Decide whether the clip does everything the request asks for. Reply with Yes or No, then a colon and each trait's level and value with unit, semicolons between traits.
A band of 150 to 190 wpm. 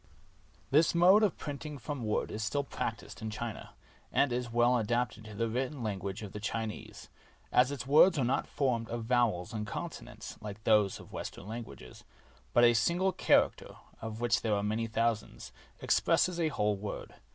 Yes: average, 175 wpm